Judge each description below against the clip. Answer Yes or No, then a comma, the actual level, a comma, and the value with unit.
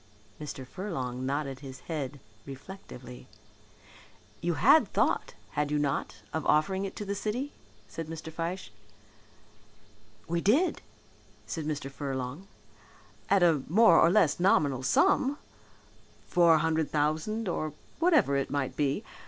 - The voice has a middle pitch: Yes, medium, 155 Hz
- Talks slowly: Yes, slow, 130 wpm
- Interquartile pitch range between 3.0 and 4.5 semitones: No, wide, 5.5 semitones